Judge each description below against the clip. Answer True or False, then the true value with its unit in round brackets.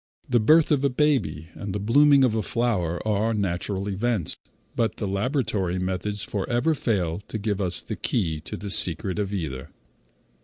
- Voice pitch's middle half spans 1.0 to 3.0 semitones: False (4.4 semitones)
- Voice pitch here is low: True (105 Hz)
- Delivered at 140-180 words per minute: True (175 wpm)